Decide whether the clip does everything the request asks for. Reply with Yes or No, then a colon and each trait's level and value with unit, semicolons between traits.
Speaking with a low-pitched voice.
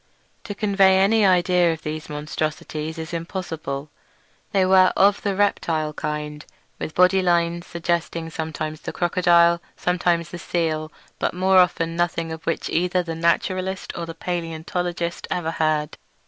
No: medium, 170 Hz